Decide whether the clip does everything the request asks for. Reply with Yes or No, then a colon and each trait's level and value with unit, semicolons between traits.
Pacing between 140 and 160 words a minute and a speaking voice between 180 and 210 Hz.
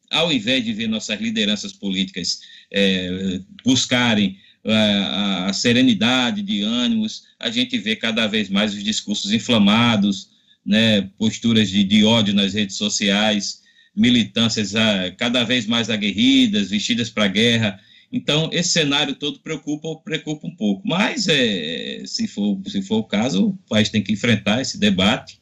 Yes: average, 150 wpm; high, 190 Hz